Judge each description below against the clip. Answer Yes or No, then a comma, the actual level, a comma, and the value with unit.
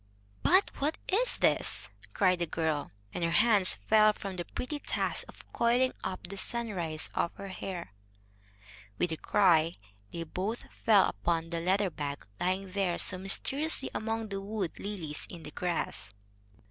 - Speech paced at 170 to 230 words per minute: No, average, 160 wpm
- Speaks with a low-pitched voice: No, medium, 185 Hz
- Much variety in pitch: No, average, 4.2 semitones